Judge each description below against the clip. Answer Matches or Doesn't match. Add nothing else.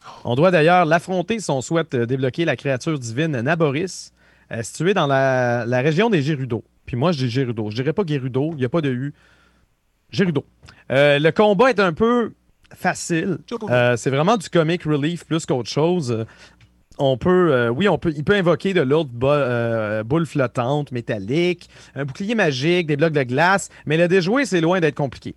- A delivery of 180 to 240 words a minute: Matches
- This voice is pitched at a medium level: Matches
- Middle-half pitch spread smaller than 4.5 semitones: Doesn't match